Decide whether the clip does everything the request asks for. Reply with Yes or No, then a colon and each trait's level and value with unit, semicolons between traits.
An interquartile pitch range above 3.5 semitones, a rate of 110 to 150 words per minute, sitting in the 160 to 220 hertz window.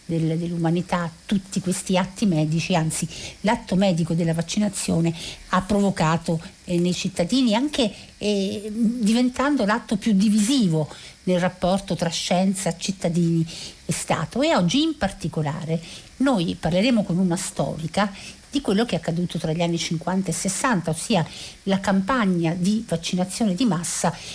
Yes: average, 3.9 semitones; average, 135 wpm; medium, 185 Hz